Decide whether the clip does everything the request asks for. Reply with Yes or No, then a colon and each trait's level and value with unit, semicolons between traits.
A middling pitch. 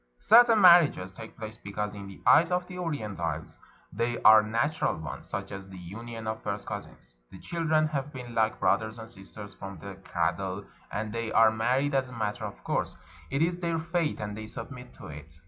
No: low, 110 Hz